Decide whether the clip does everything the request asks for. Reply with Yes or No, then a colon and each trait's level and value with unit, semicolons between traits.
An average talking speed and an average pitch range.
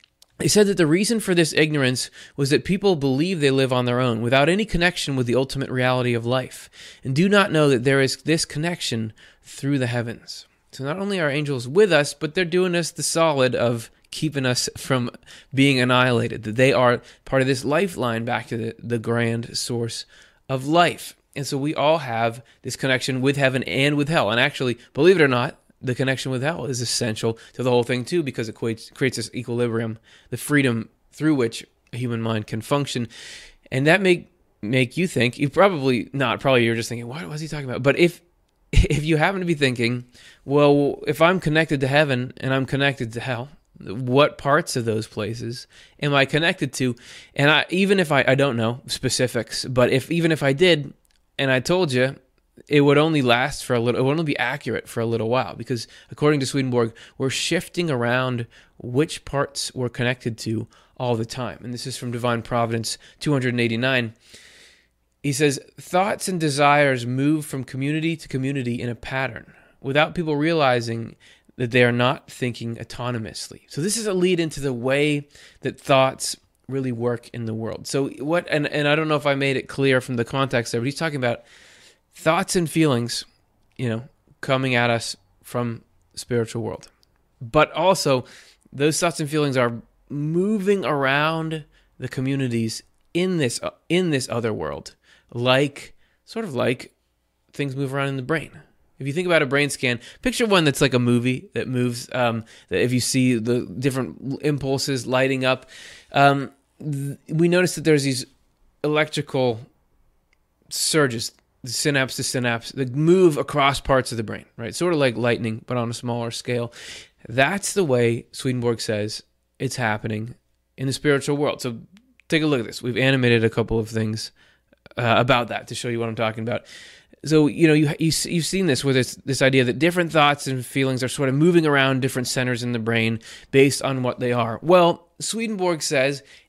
Yes: average, 190 wpm; average, 3.8 semitones